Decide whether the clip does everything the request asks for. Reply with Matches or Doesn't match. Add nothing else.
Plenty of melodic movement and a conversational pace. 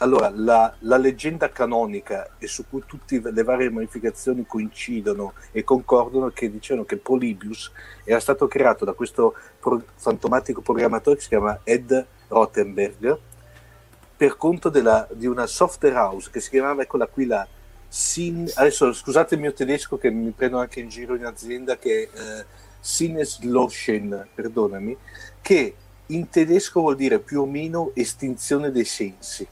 Doesn't match